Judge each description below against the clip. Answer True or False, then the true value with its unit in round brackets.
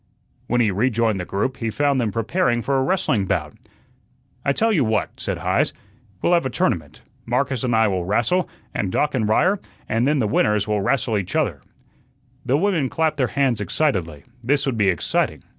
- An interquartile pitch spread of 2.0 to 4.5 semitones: False (5.2 semitones)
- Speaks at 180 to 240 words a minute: True (190 wpm)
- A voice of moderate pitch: False (120 Hz)